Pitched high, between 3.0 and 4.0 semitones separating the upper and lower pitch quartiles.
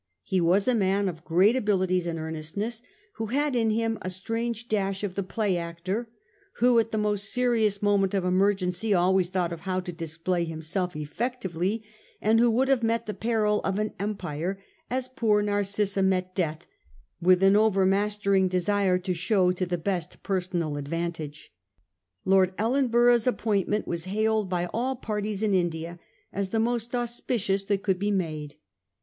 Yes: high, 195 Hz; average, 3.4 semitones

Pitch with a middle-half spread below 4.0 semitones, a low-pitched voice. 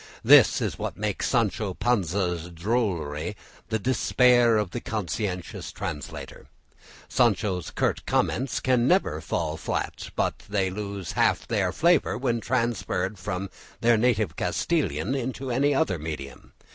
No: average, 5.3 semitones; low, 105 Hz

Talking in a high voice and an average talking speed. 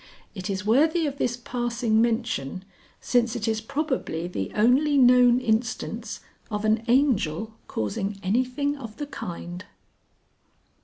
No: high, 230 Hz; slow, 125 wpm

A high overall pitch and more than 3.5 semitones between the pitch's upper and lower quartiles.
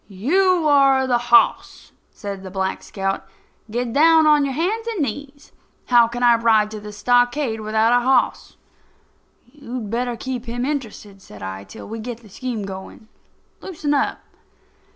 Yes: high, 240 Hz; average, 4.6 semitones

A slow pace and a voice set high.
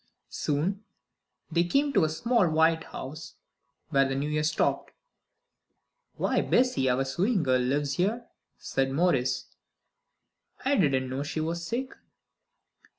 No: slow, 130 wpm; medium, 155 Hz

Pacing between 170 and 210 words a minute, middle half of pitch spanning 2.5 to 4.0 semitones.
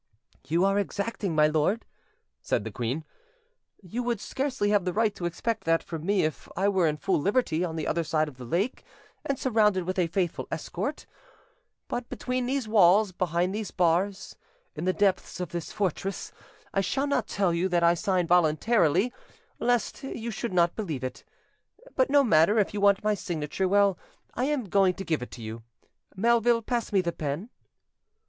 No: average, 185 wpm; average, 4.6 semitones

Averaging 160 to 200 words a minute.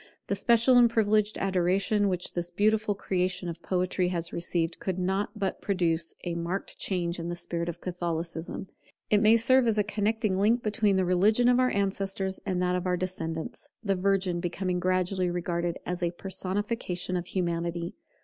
Yes: average, 175 wpm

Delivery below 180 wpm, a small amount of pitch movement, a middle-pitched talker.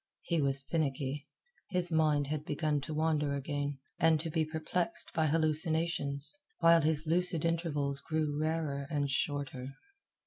Yes: average, 140 wpm; narrow, 2.2 semitones; medium, 155 Hz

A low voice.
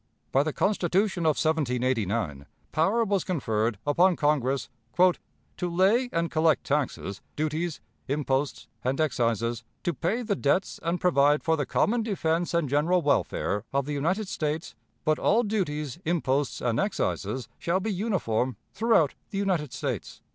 No: medium, 155 Hz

